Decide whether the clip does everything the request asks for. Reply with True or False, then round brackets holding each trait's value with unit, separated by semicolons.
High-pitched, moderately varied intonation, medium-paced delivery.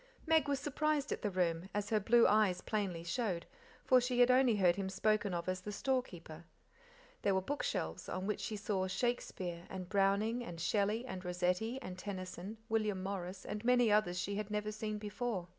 True (205 Hz; 3.6 semitones; 190 wpm)